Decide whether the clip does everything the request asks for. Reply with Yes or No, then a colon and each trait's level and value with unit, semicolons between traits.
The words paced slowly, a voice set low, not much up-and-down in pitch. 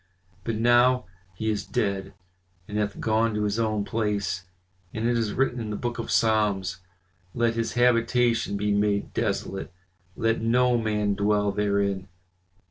No: average, 155 wpm; low, 110 Hz; narrow, 2.2 semitones